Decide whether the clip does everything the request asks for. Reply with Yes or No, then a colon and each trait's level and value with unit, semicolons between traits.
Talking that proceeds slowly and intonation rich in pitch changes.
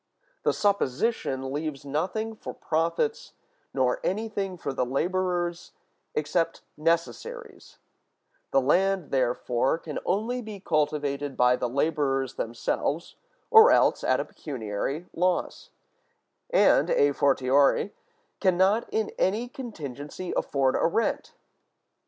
Yes: slow, 110 wpm; wide, 6.7 semitones